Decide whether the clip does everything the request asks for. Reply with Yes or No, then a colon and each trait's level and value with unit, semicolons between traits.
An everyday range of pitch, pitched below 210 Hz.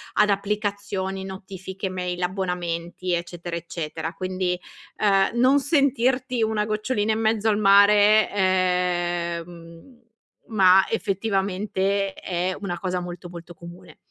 Yes: average, 3.0 semitones; high, 190 Hz